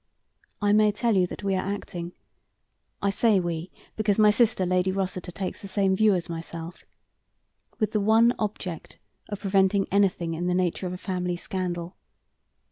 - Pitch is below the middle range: No, high, 190 Hz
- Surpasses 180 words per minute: No, average, 170 wpm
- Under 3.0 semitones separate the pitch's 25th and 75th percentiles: Yes, narrow, 2.4 semitones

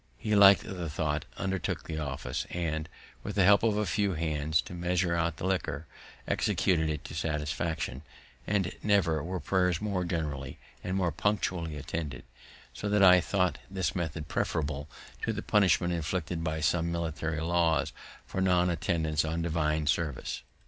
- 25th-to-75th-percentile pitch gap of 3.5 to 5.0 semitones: No, average, 2.9 semitones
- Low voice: Yes, very low, 85 Hz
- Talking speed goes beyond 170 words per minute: No, average, 160 wpm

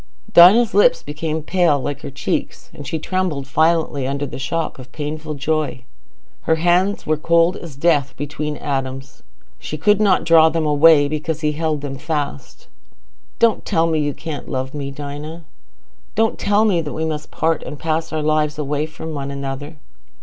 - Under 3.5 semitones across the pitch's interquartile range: Yes, narrow, 2.4 semitones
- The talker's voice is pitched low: No, medium, 155 Hz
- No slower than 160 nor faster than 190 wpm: Yes, average, 170 wpm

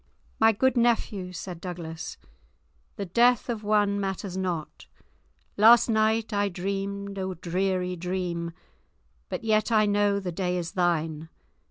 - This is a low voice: No, high, 195 Hz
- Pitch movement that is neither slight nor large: Yes, average, 3.1 semitones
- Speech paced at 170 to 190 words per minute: No, slow, 135 wpm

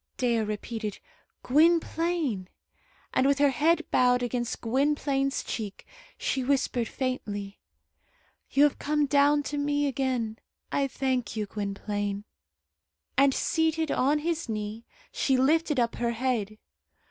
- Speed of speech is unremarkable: No, slow, 125 wpm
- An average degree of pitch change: Yes, average, 4.4 semitones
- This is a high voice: Yes, very high, 260 Hz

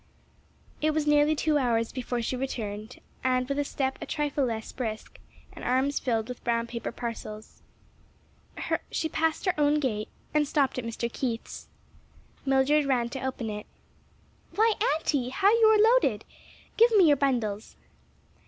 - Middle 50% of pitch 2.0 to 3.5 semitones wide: No, average, 4.2 semitones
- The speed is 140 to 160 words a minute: Yes, average, 155 wpm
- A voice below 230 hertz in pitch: No, very high, 265 Hz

